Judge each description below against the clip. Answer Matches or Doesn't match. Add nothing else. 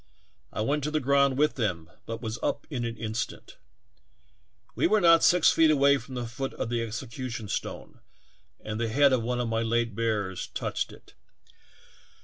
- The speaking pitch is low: Matches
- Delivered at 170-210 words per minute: Matches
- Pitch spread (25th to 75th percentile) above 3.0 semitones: Matches